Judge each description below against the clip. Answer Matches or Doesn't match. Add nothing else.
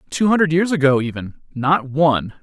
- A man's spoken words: Matches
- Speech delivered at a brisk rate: Doesn't match